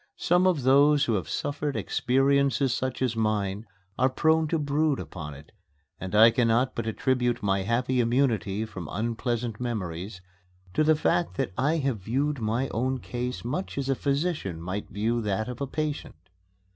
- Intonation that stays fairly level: No, average, 4.5 semitones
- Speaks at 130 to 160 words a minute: No, average, 170 wpm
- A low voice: Yes, low, 120 Hz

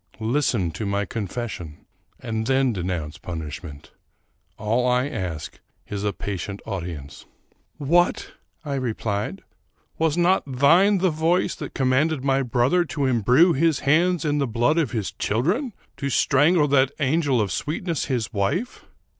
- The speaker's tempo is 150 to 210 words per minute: Yes, average, 160 wpm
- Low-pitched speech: Yes, low, 130 Hz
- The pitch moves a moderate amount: No, wide, 7.0 semitones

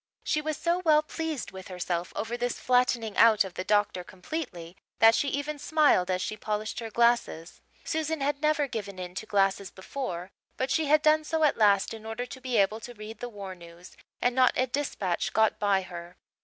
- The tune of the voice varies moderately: No, wide, 6.6 semitones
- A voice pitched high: Yes, high, 225 Hz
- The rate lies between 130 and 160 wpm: No, fast, 205 wpm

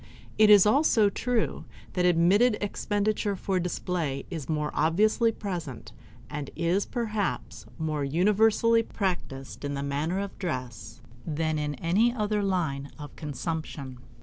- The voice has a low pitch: No, medium, 180 Hz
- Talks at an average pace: No, slow, 130 wpm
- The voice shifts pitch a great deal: Yes, wide, 5.7 semitones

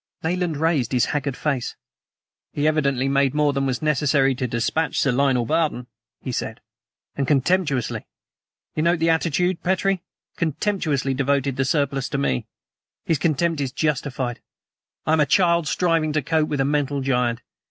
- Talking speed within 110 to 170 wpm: Yes, average, 160 wpm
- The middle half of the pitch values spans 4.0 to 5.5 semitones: No, average, 3.2 semitones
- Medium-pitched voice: Yes, medium, 145 Hz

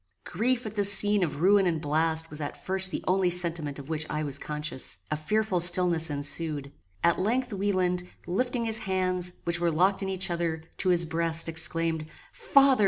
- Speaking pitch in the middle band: Yes, medium, 175 Hz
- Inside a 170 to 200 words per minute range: Yes, average, 185 wpm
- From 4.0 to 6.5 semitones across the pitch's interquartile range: No, average, 3.2 semitones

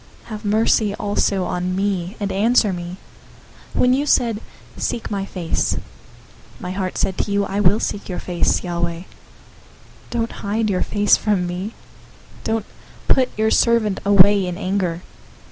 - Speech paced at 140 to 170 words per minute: Yes, average, 155 wpm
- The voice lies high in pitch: Yes, high, 200 Hz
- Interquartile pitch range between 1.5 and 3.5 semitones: Yes, average, 3.0 semitones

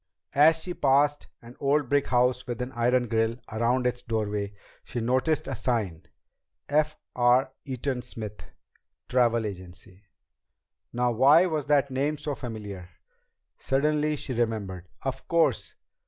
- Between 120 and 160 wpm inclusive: Yes, slow, 135 wpm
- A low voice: Yes, low, 125 Hz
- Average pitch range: Yes, average, 4.0 semitones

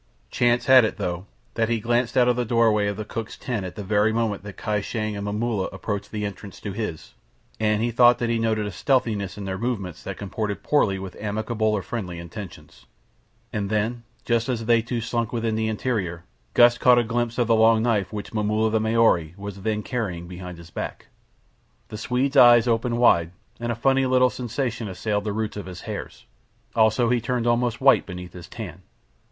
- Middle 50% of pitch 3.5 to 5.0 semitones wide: No, average, 2.7 semitones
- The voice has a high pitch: No, low, 110 Hz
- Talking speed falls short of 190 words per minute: No, fast, 205 wpm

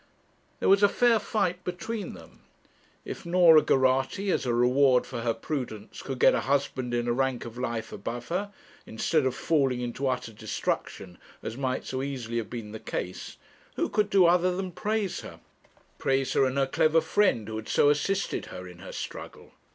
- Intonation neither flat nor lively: No, wide, 6.9 semitones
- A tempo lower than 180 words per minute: No, average, 190 wpm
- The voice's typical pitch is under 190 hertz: Yes, low, 135 Hz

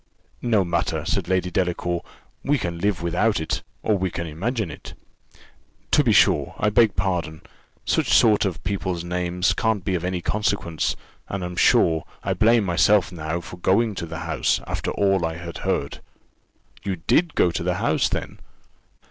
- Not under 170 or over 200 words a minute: Yes, average, 175 wpm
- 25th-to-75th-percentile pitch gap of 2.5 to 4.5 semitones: Yes, average, 3.1 semitones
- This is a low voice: Yes, very low, 90 Hz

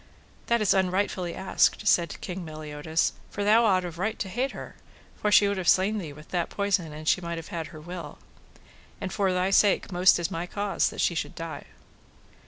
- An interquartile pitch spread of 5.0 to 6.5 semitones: No, average, 3.3 semitones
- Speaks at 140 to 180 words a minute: No, fast, 205 wpm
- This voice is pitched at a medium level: Yes, medium, 180 Hz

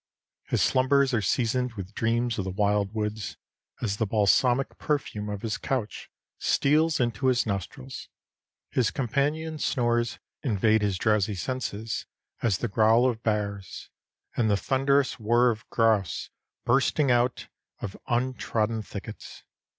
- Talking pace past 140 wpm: No, slow, 135 wpm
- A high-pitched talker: No, low, 115 Hz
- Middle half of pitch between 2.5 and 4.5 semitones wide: Yes, average, 3.5 semitones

